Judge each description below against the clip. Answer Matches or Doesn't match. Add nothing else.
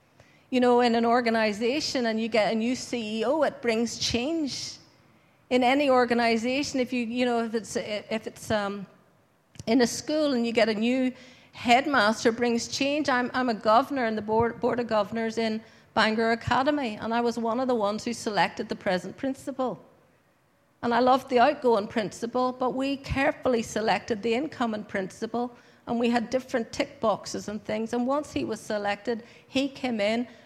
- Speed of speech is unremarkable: Matches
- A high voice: Matches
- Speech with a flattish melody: Matches